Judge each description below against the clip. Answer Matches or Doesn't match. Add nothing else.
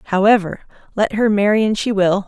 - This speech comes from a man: Doesn't match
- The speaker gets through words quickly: Doesn't match